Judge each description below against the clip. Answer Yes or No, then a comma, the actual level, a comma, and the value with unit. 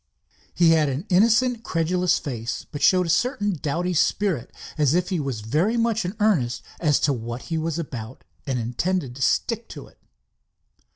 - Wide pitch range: Yes, wide, 5.7 semitones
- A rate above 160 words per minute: Yes, average, 175 wpm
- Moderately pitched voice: Yes, medium, 165 Hz